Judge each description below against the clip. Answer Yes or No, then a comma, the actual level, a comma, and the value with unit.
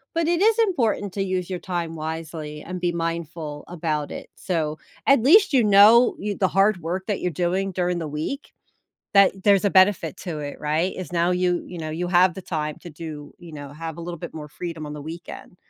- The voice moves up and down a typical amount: Yes, average, 3.5 semitones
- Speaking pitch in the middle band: Yes, medium, 175 Hz